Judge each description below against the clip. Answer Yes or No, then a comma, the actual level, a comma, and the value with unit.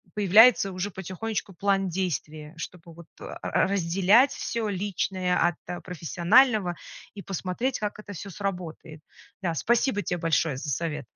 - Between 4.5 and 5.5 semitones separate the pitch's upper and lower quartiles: No, average, 3.4 semitones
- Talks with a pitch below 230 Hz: Yes, medium, 185 Hz